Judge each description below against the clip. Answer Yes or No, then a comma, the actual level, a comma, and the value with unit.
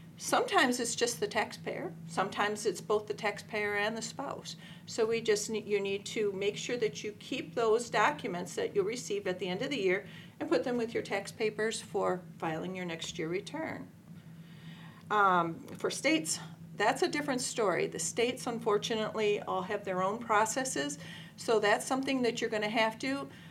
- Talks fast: No, average, 185 wpm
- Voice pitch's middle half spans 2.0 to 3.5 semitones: No, average, 4.0 semitones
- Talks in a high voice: Yes, high, 205 Hz